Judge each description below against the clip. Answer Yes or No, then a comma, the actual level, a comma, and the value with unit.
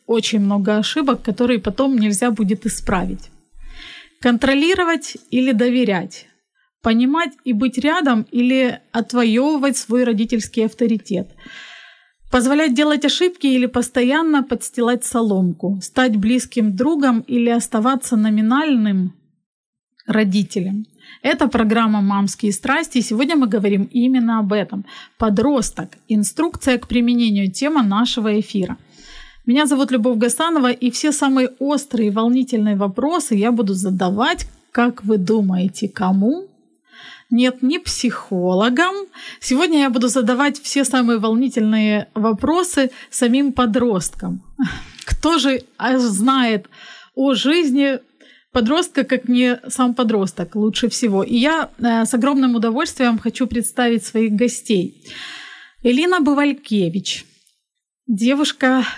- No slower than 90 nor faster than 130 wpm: Yes, average, 110 wpm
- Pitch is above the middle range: Yes, high, 245 Hz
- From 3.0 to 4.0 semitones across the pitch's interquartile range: Yes, average, 3.7 semitones